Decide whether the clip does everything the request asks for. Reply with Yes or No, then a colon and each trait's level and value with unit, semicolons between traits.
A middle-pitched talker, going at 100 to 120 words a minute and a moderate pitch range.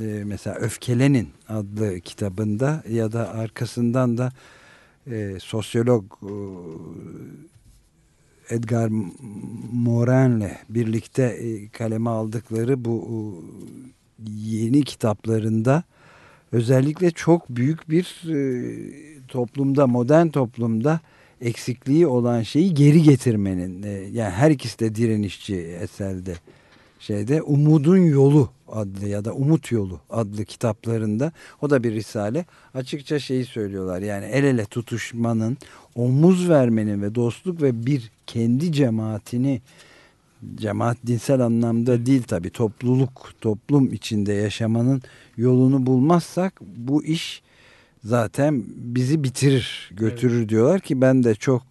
No: low, 120 Hz; average, 110 wpm; average, 3.9 semitones